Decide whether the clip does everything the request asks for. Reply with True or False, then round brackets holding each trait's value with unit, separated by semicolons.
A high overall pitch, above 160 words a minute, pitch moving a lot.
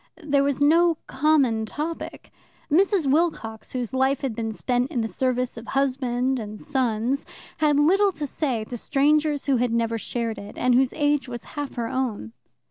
False (265 Hz; 175 wpm; 3.8 semitones)